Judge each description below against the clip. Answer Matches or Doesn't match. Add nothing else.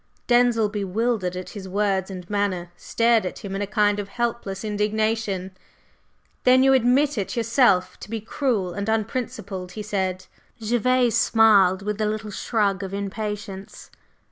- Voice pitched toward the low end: Doesn't match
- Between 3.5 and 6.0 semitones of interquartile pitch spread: Doesn't match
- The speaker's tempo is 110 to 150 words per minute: Matches